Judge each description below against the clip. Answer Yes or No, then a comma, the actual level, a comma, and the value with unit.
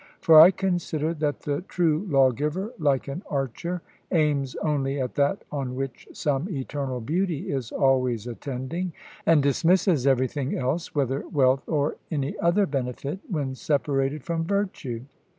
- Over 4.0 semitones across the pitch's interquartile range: No, average, 3.6 semitones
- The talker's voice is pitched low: No, medium, 145 Hz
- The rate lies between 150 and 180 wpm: No, average, 140 wpm